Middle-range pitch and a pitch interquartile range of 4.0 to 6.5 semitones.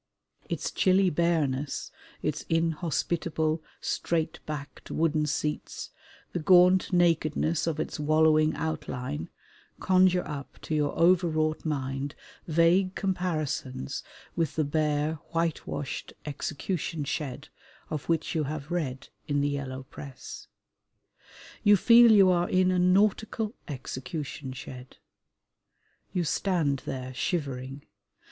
No: medium, 155 Hz; average, 3.5 semitones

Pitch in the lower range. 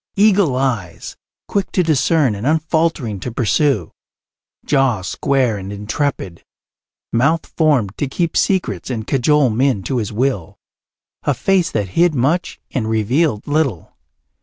Yes: low, 130 Hz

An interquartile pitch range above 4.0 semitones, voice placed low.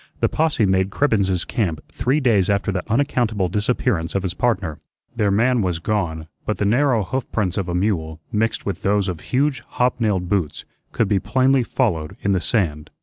Yes: average, 4.6 semitones; low, 100 Hz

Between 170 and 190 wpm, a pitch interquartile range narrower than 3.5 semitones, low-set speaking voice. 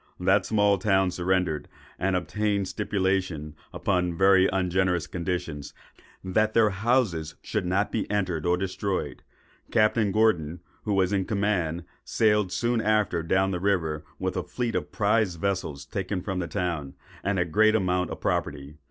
No: average, 155 wpm; average, 2.7 semitones; very low, 95 Hz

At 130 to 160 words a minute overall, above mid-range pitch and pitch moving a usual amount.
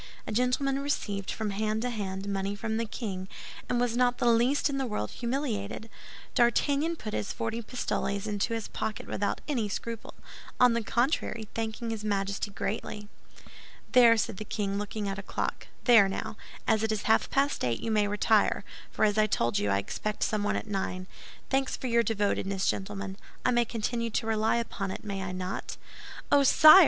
No: average, 185 wpm; high, 220 Hz; average, 3.0 semitones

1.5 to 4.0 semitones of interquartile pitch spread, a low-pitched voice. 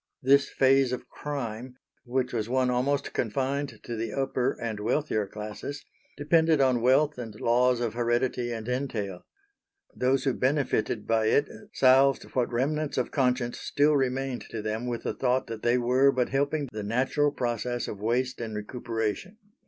Yes: average, 2.7 semitones; low, 125 Hz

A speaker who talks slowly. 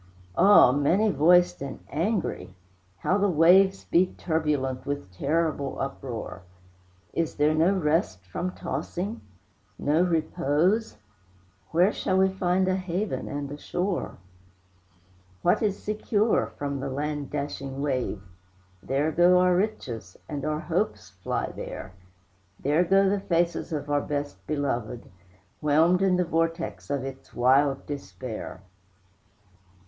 Yes: slow, 125 wpm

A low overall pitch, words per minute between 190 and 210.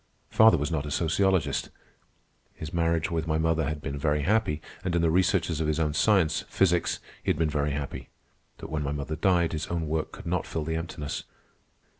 Yes: very low, 80 Hz; average, 200 wpm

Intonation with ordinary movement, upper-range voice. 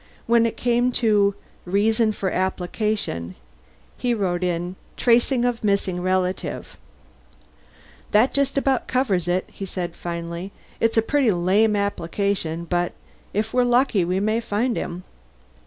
Yes: average, 4.5 semitones; high, 200 Hz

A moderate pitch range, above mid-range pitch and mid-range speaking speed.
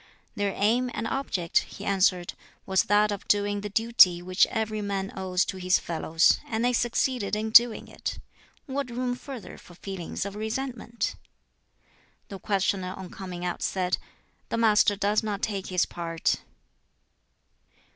Yes: average, 3.3 semitones; high, 205 Hz; average, 150 wpm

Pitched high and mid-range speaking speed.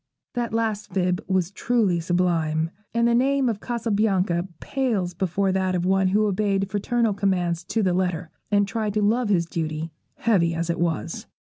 Yes: high, 195 Hz; average, 170 wpm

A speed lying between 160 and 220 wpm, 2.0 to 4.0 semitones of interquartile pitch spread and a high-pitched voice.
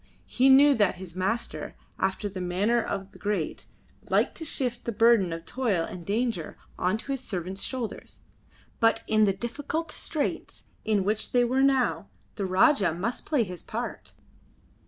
No: average, 165 wpm; average, 5.0 semitones; high, 215 Hz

